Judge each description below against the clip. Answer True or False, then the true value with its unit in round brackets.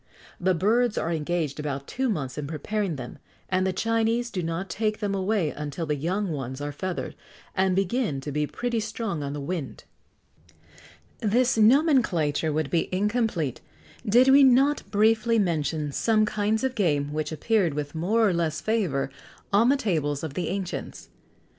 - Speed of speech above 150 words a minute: True (170 wpm)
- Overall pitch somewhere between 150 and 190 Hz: True (185 Hz)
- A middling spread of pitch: False (6.7 semitones)